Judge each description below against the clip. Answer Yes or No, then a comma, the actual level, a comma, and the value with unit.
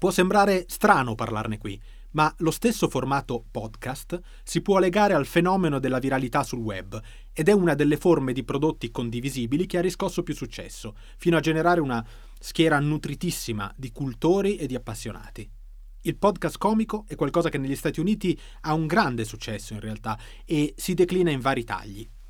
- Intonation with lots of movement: Yes, wide, 6.9 semitones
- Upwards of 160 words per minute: Yes, fast, 170 wpm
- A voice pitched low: No, medium, 145 Hz